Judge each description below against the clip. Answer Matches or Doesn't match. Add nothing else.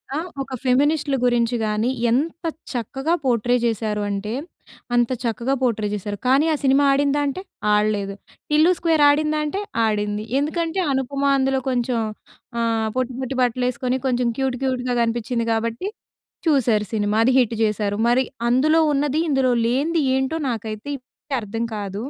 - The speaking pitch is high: Matches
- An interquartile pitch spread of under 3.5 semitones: Doesn't match